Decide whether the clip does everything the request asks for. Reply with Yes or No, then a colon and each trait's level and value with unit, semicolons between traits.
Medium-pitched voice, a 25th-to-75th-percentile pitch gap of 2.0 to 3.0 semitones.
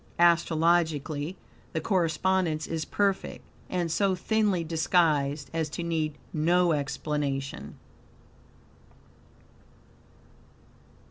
Yes: medium, 165 Hz; narrow, 2.6 semitones